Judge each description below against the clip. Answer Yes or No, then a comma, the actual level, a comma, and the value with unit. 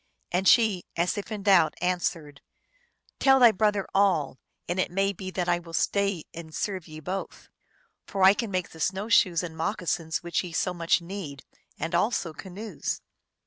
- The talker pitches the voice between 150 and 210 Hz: Yes, medium, 185 Hz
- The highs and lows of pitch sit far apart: No, average, 3.1 semitones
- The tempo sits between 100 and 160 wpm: No, average, 185 wpm